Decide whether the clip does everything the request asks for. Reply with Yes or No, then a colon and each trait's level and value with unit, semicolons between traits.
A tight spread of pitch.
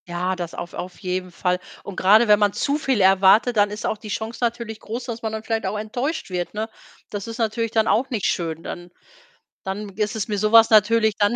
No: average, 3.0 semitones